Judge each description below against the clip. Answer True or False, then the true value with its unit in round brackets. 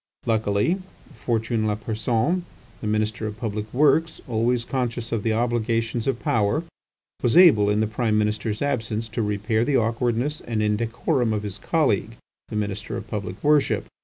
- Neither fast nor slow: True (155 wpm)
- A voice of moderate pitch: False (115 Hz)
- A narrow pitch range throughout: True (2.3 semitones)